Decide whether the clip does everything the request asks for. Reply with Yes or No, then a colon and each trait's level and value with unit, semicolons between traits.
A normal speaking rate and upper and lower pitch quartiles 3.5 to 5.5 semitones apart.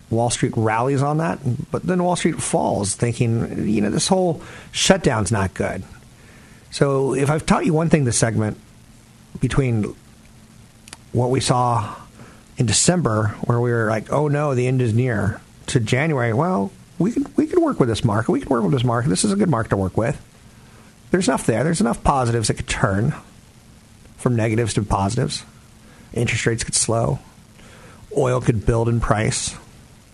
Yes: average, 180 wpm; average, 4.4 semitones